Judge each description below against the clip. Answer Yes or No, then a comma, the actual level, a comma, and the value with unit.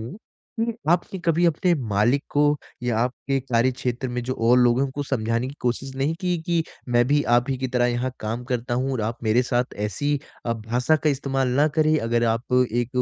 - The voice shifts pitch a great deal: No, average, 2.8 semitones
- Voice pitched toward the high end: No, low, 125 Hz